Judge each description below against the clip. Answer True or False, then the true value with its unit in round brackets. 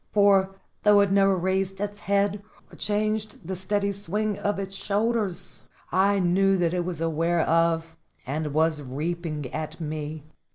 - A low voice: False (190 Hz)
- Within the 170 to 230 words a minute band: False (155 wpm)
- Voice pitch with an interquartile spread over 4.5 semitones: False (3.5 semitones)